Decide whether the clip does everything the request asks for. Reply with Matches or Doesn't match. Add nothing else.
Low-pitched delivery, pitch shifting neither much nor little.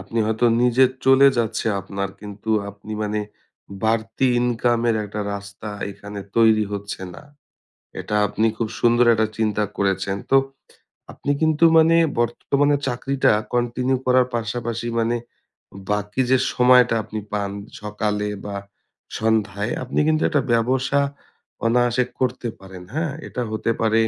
Matches